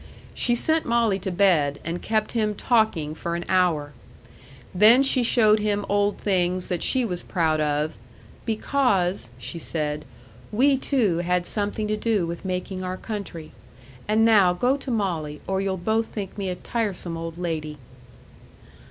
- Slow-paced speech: No, average, 160 wpm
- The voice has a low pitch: No, high, 190 Hz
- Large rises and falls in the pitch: No, average, 4.3 semitones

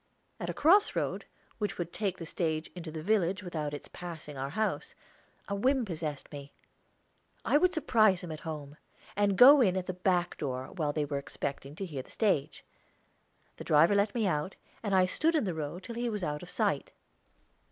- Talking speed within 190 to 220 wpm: Yes, average, 200 wpm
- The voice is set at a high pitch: No, medium, 180 Hz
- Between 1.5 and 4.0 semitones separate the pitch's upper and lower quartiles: No, average, 5.3 semitones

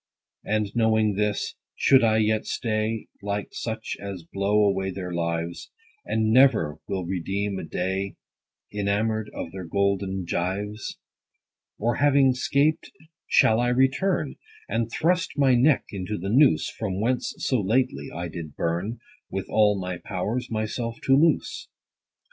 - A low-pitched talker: Yes, low, 105 Hz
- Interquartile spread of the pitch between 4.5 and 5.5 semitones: No, average, 3.7 semitones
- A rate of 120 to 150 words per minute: Yes, average, 140 wpm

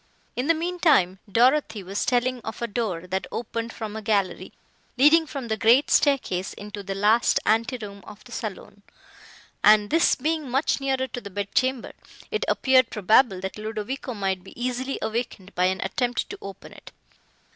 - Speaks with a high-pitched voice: Yes, high, 230 Hz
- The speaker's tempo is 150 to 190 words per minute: Yes, average, 180 wpm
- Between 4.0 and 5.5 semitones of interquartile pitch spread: Yes, average, 4.4 semitones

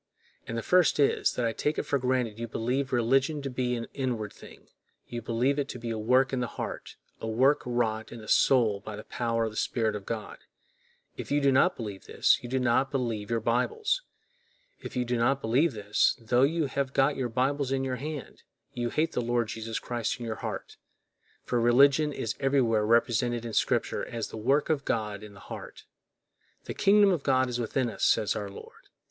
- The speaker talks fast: Yes, fast, 210 wpm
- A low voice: Yes, low, 120 Hz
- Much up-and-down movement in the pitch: No, average, 3.1 semitones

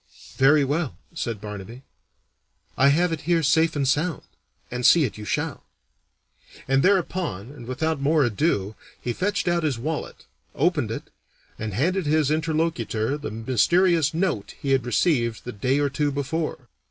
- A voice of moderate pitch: Yes, medium, 145 Hz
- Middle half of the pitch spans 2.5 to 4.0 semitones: No, average, 5.0 semitones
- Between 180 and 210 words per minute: No, average, 155 wpm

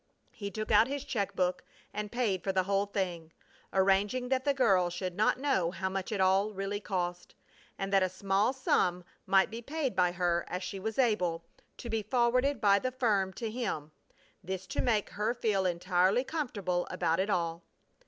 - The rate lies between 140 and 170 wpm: No, average, 190 wpm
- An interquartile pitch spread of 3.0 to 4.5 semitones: Yes, average, 3.8 semitones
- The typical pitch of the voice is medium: No, high, 195 Hz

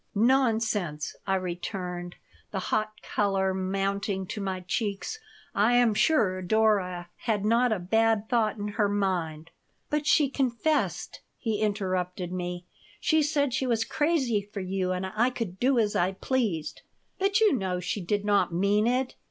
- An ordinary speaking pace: Yes, average, 160 wpm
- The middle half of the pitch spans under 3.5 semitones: No, average, 4.0 semitones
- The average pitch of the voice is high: Yes, high, 205 Hz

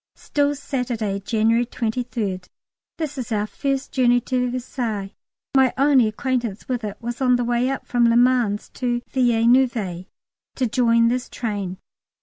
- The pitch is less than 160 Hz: No, high, 240 Hz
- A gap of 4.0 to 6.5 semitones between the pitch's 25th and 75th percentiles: No, narrow, 2.5 semitones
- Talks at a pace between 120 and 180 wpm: Yes, average, 145 wpm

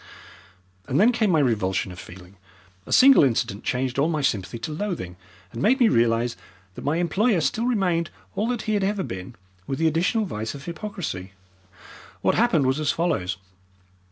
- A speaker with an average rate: Yes, average, 180 wpm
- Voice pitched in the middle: Yes, medium, 155 Hz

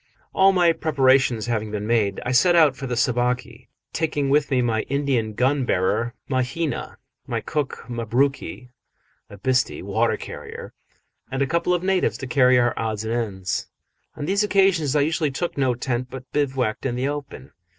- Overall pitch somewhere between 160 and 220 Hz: No, low, 130 Hz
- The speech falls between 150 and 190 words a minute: Yes, average, 170 wpm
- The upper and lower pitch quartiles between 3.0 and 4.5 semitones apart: Yes, average, 3.7 semitones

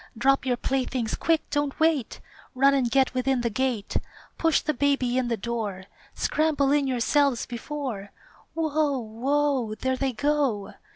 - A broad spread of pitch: No, average, 3.3 semitones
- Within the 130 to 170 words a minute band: Yes, average, 150 wpm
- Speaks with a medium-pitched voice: No, very high, 265 Hz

